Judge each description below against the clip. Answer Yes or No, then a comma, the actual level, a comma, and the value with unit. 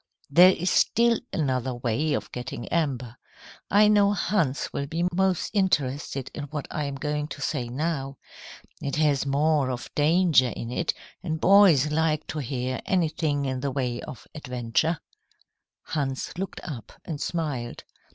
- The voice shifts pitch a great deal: No, average, 4.2 semitones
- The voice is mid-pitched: Yes, medium, 145 Hz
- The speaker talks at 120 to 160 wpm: Yes, average, 150 wpm